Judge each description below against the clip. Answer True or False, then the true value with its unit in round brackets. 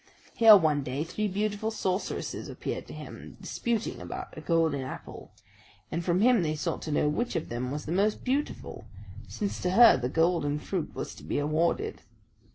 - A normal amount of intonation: False (6.0 semitones)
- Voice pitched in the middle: True (170 Hz)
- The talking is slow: False (180 wpm)